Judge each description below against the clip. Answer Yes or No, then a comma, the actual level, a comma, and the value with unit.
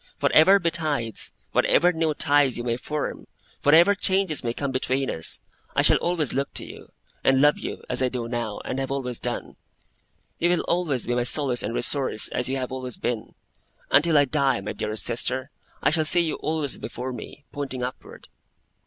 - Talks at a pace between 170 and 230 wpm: Yes, average, 190 wpm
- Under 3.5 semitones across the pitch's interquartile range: No, average, 3.9 semitones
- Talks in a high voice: No, low, 135 Hz